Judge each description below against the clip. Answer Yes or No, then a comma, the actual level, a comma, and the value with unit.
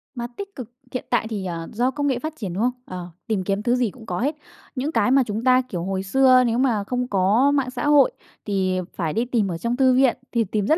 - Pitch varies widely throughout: No, average, 4.6 semitones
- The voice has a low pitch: No, high, 240 Hz